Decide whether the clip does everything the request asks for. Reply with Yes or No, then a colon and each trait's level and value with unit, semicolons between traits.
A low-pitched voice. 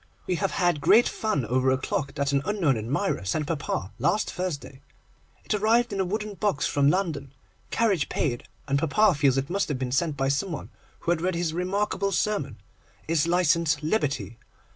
No: medium, 160 Hz